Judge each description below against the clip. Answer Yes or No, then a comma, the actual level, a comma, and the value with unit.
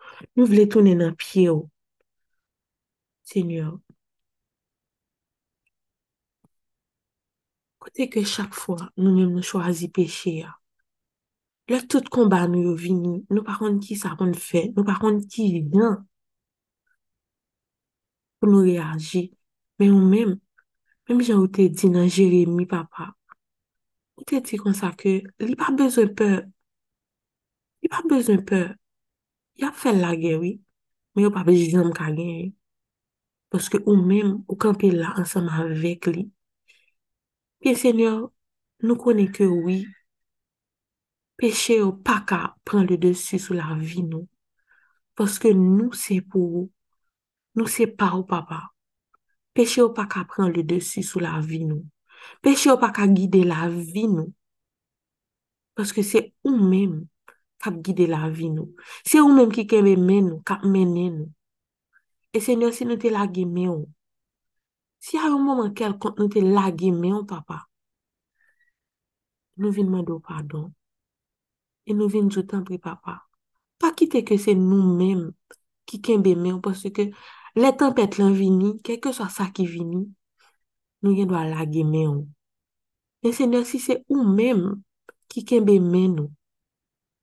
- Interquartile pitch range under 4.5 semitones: Yes, average, 3.9 semitones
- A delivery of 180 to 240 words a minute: No, average, 150 wpm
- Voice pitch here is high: Yes, high, 195 Hz